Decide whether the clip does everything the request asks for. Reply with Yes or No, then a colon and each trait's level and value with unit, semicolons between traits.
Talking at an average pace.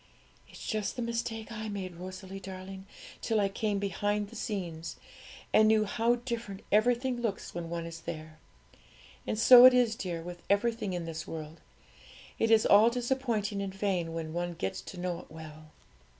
Yes: average, 175 wpm